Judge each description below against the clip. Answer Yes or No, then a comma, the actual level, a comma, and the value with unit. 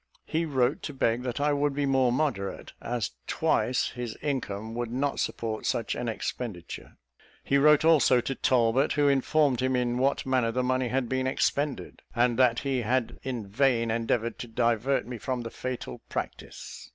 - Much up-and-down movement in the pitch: No, narrow, 2.6 semitones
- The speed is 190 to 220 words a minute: No, average, 175 wpm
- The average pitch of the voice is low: Yes, low, 125 Hz